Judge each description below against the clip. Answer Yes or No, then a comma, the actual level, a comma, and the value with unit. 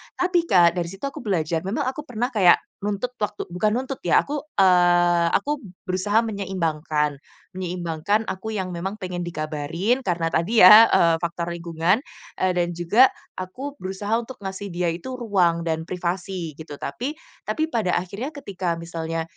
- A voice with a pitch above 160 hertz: Yes, medium, 185 Hz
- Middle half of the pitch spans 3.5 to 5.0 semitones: Yes, average, 4.3 semitones